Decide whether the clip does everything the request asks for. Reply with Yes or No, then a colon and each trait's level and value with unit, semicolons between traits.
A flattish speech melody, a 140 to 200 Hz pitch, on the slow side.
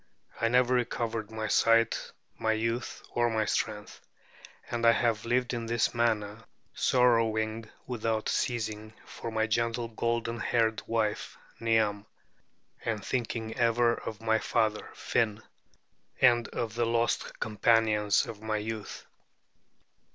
No: narrow, 1.3 semitones; low, 115 Hz; slow, 125 wpm